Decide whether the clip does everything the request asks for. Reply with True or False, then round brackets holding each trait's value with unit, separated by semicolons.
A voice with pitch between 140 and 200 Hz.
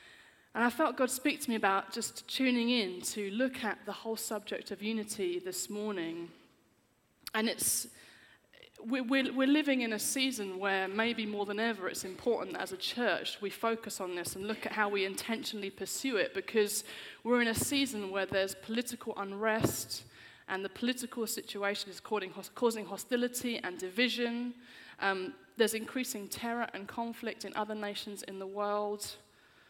False (220 Hz)